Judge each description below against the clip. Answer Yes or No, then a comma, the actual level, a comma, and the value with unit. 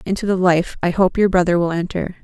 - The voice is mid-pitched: Yes, medium, 180 Hz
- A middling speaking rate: No, fast, 240 wpm